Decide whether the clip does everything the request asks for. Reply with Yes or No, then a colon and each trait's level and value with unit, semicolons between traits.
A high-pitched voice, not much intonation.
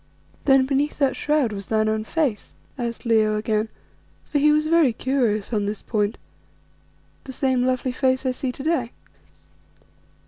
No: very high, 255 Hz; average, 4.2 semitones